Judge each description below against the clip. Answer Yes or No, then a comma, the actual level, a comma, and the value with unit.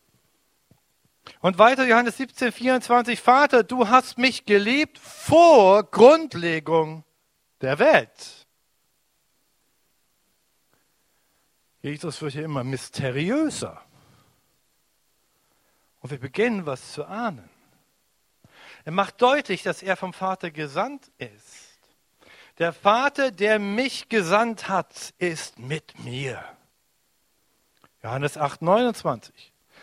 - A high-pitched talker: Yes, high, 195 Hz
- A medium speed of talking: No, slow, 95 wpm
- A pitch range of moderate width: No, wide, 7.7 semitones